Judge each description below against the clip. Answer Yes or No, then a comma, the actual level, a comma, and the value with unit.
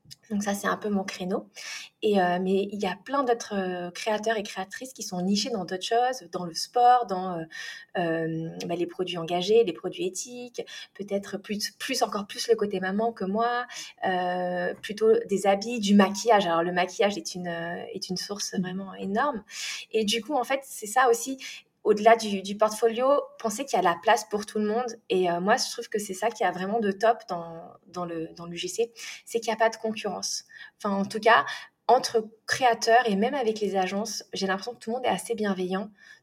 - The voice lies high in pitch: Yes, high, 210 Hz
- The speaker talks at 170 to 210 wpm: No, fast, 220 wpm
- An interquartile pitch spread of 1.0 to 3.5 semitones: No, average, 4.0 semitones